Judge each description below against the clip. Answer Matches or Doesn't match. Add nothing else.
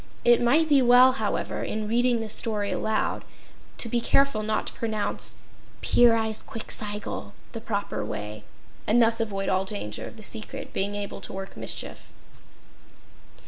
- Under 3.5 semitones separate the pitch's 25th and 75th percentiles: Matches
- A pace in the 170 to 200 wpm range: Doesn't match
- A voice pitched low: Doesn't match